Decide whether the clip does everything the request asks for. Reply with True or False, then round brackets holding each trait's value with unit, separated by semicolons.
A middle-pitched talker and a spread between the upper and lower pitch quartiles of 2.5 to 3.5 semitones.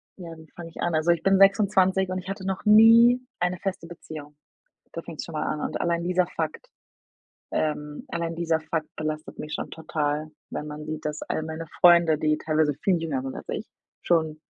True (165 Hz; 2.9 semitones)